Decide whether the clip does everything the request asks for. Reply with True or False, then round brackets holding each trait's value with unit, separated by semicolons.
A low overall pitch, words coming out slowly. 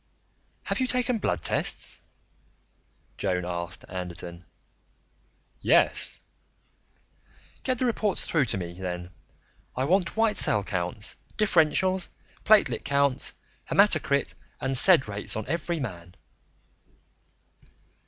True (130 Hz; 105 wpm)